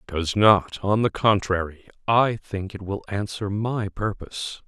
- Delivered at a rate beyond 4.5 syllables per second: No, 4.3 syllables/s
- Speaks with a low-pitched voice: Yes, low, 100 Hz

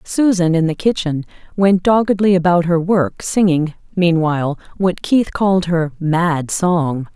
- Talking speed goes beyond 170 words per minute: No, average, 145 wpm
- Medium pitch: Yes, medium, 175 Hz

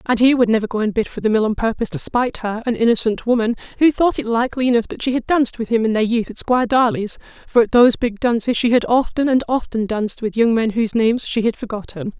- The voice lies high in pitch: Yes, high, 235 Hz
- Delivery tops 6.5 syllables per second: Yes, 6.7 syllables/s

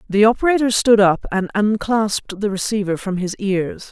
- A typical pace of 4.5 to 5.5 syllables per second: Yes, 5.0 syllables/s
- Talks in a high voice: Yes, high, 205 Hz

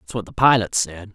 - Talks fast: Yes, fast, 260 wpm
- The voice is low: Yes, low, 105 Hz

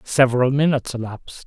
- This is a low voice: Yes, low, 130 Hz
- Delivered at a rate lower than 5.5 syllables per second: No, 6.7 syllables/s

